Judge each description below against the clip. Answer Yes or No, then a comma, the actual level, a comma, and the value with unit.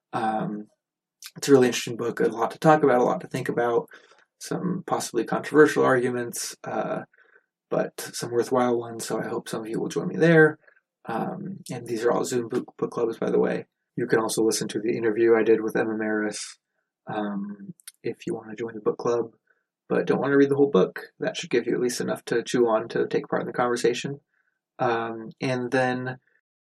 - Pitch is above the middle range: No, low, 125 Hz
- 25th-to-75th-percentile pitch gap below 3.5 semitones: No, average, 3.8 semitones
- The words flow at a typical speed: No, fast, 215 wpm